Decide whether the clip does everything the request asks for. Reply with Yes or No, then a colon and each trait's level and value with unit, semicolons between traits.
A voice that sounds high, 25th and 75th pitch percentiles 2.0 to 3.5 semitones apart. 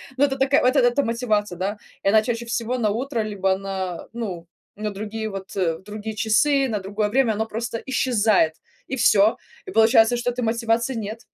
Yes: high, 220 Hz; average, 2.8 semitones